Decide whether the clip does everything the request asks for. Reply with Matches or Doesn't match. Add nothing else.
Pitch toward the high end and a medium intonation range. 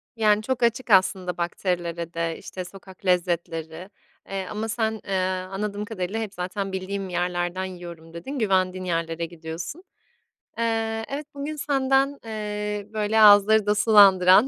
Matches